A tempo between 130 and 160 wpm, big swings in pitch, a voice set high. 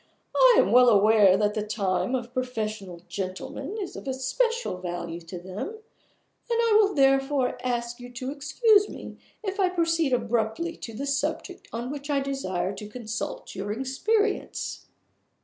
Yes: average, 155 wpm; wide, 7.7 semitones; very high, 255 Hz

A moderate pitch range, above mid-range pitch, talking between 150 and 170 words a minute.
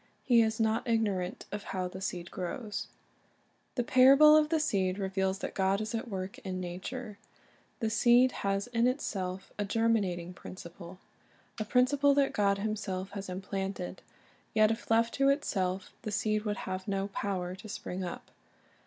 Yes: average, 3.4 semitones; high, 205 Hz; average, 160 wpm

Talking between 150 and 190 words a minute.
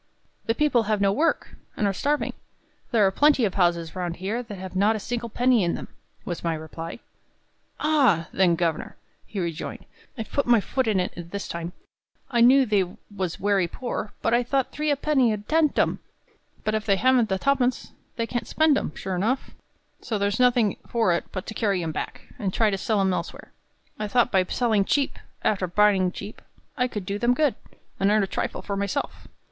No: fast, 205 wpm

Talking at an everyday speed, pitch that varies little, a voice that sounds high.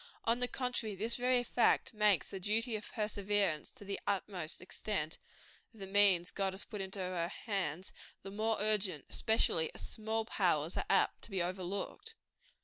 No: average, 170 wpm; average, 3.0 semitones; high, 200 Hz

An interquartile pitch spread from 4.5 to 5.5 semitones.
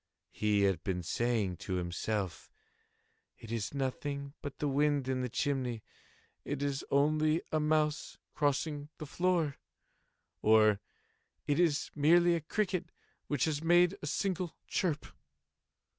Yes: average, 5.1 semitones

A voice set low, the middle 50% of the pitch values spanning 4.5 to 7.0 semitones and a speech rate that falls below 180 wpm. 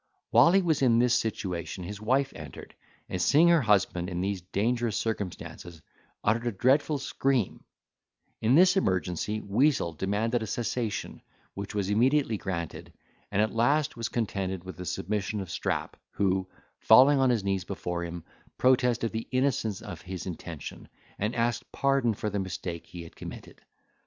Yes: low, 110 Hz; average, 4.9 semitones; average, 160 wpm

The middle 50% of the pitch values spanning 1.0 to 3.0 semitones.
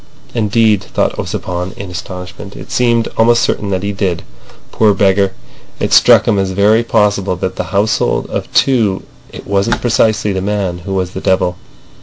Yes: narrow, 2.5 semitones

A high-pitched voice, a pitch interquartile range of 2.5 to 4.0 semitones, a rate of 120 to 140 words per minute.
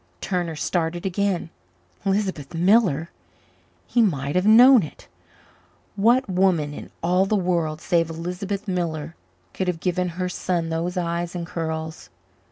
No: medium, 175 Hz; average, 2.8 semitones; slow, 135 wpm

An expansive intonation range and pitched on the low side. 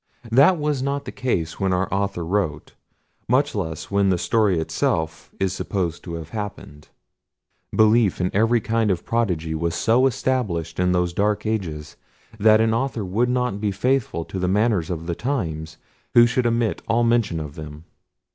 Yes: wide, 5.8 semitones; low, 100 Hz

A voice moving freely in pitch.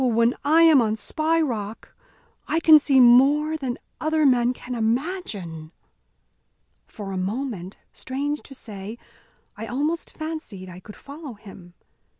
Yes: wide, 6.2 semitones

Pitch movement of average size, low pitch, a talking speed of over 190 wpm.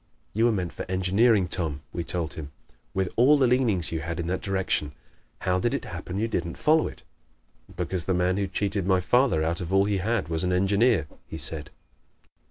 Yes: average, 3.6 semitones; very low, 95 Hz; fast, 205 wpm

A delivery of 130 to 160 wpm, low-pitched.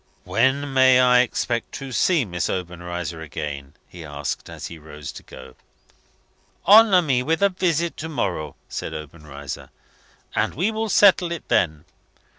Yes: average, 150 wpm; low, 120 Hz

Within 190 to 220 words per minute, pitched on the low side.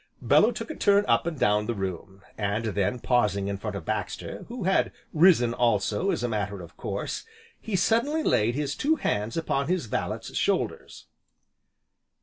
No: average, 170 wpm; low, 115 Hz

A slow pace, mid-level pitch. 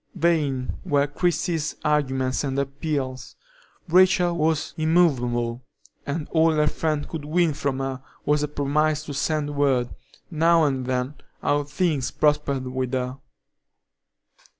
Yes: slow, 125 wpm; medium, 145 Hz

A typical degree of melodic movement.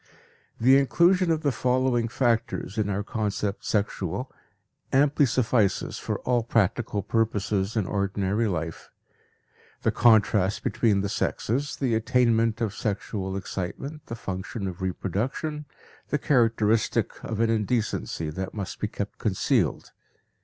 Yes: average, 4.0 semitones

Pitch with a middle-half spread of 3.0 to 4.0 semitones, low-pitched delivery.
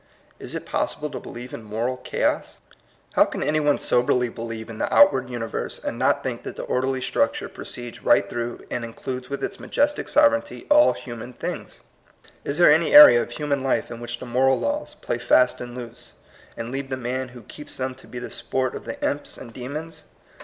Yes: average, 3.4 semitones; low, 130 Hz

